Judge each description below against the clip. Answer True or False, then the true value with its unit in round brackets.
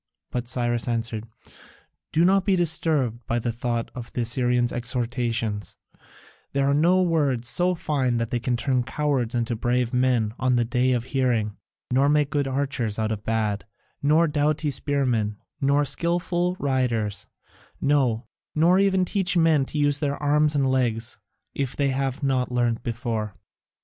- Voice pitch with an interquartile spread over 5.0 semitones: False (3.8 semitones)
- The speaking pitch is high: False (130 Hz)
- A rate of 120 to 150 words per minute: False (160 wpm)